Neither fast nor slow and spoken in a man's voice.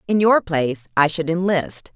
No: average, 185 wpm; female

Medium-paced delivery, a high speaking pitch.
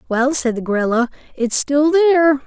Yes: average, 170 wpm; very high, 275 Hz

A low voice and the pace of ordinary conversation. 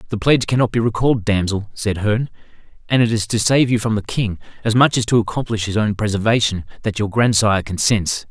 No: low, 110 Hz; fast, 210 wpm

